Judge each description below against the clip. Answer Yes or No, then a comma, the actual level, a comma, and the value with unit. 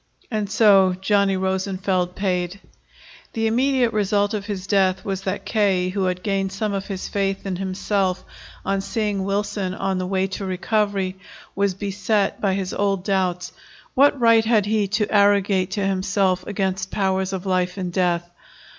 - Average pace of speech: Yes, average, 165 wpm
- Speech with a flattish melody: Yes, narrow, 1.5 semitones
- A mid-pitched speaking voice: No, high, 195 Hz